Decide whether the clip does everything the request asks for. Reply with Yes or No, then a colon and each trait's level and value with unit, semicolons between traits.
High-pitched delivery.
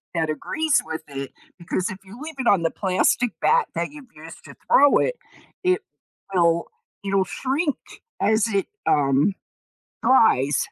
Yes: high, 195 Hz